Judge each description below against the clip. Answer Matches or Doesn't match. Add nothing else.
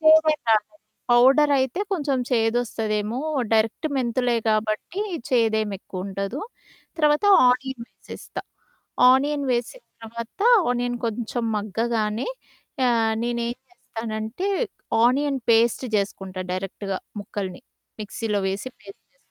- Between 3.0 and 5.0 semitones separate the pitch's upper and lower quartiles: Matches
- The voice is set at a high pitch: Matches